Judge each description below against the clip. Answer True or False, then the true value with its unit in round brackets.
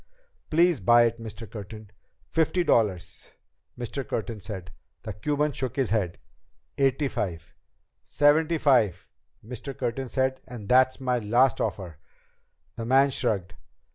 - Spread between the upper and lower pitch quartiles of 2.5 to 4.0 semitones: False (4.5 semitones)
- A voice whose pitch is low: True (120 Hz)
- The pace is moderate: False (130 wpm)